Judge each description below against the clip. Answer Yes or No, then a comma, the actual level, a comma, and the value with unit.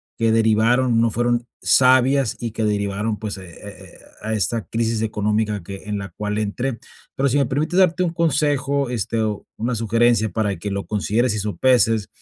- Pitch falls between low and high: No, low, 115 Hz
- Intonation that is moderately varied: Yes, average, 3.1 semitones